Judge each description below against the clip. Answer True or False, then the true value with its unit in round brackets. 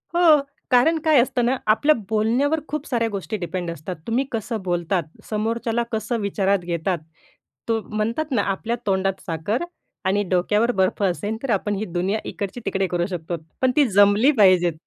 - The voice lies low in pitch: False (210 Hz)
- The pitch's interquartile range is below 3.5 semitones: False (4.1 semitones)